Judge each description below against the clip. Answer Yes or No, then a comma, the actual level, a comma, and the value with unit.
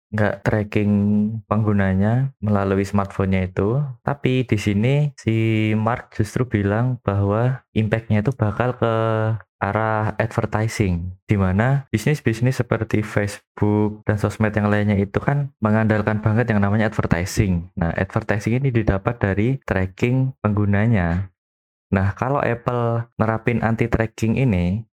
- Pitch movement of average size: No, narrow, 2.3 semitones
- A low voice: Yes, low, 110 Hz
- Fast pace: No, average, 120 wpm